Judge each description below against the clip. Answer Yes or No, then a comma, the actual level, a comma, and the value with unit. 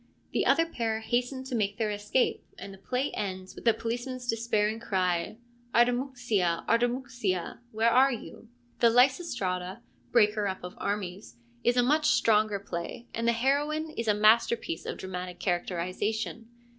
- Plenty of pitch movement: No, average, 3.7 semitones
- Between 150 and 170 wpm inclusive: Yes, average, 160 wpm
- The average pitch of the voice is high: Yes, high, 225 Hz